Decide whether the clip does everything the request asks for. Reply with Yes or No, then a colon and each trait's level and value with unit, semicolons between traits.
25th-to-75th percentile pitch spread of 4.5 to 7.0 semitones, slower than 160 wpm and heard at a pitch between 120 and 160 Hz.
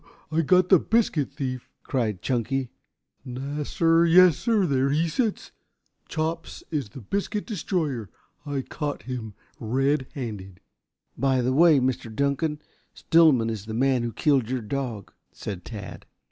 Yes: average, 5.2 semitones; average, 140 wpm; low, 135 Hz